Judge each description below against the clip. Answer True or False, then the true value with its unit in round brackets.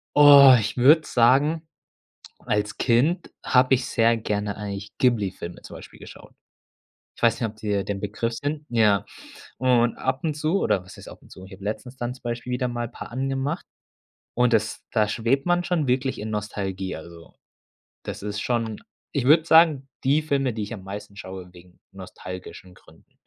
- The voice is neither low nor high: False (115 Hz)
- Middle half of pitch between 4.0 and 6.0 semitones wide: True (4.6 semitones)